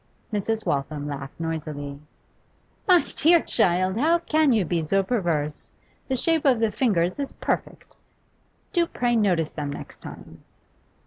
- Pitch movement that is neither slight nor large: No, wide, 8.9 semitones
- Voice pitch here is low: No, high, 195 Hz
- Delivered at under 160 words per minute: Yes, average, 140 wpm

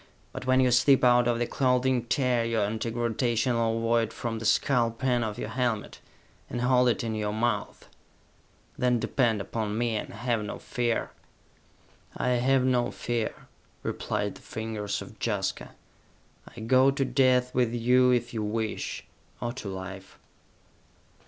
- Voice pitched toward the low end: Yes, low, 120 Hz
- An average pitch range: No, narrow, 2.0 semitones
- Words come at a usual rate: Yes, average, 155 wpm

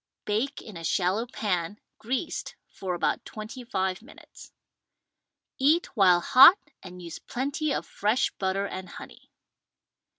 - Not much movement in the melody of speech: No, wide, 5.6 semitones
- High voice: Yes, high, 210 Hz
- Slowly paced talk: Yes, slow, 130 wpm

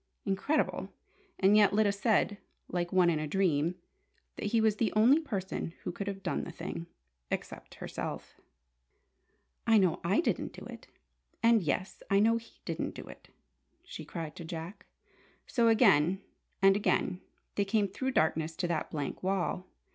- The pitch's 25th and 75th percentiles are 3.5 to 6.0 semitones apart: Yes, average, 3.8 semitones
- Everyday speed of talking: Yes, average, 160 wpm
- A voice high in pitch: Yes, high, 195 Hz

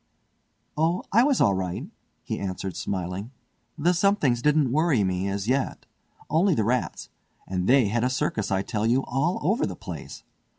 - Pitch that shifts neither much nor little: No, wide, 8.1 semitones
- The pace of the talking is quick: No, average, 170 wpm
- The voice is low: Yes, low, 125 Hz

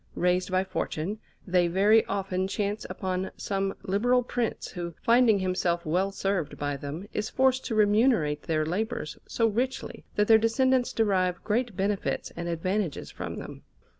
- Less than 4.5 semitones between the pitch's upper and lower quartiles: Yes, average, 3.7 semitones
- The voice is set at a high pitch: Yes, high, 195 Hz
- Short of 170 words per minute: Yes, average, 155 wpm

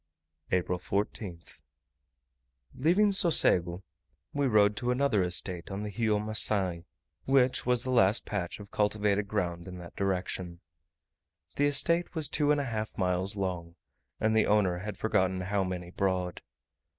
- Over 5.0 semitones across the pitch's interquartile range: No, average, 4.6 semitones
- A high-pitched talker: No, low, 100 Hz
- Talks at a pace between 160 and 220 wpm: No, average, 145 wpm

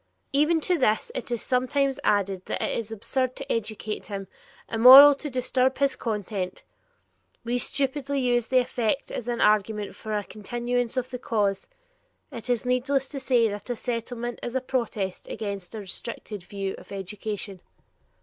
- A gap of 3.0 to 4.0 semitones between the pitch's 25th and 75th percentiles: Yes, average, 3.6 semitones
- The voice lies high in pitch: Yes, high, 235 Hz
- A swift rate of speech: No, average, 170 wpm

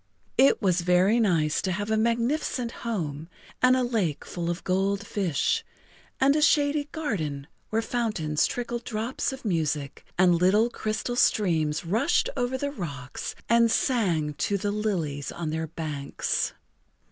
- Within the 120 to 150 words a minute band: Yes, average, 145 wpm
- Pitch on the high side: Yes, high, 200 Hz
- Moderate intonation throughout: No, wide, 6.7 semitones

